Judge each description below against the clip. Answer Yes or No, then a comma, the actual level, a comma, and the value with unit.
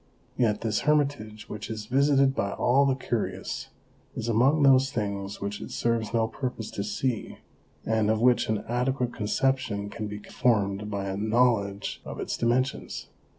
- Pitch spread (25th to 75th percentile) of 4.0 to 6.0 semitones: No, average, 3.6 semitones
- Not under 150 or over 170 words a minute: Yes, average, 160 wpm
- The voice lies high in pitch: No, low, 115 Hz